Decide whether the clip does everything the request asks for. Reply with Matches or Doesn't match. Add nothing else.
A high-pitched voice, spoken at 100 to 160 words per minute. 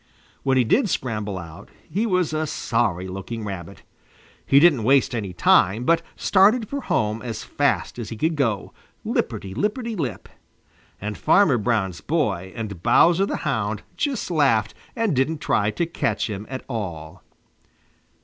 Doesn't match